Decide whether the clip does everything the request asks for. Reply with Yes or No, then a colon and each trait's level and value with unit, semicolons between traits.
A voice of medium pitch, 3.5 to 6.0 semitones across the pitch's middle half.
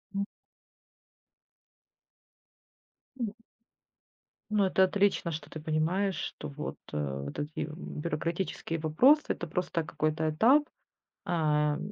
Yes: medium, 165 Hz; average, 4.1 semitones